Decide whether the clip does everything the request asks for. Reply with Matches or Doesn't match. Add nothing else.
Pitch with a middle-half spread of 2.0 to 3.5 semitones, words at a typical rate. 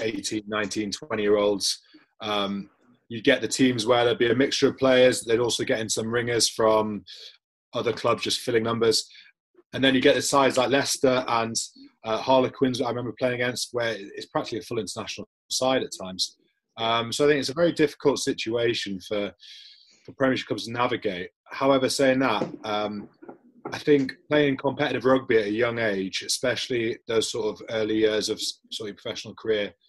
Doesn't match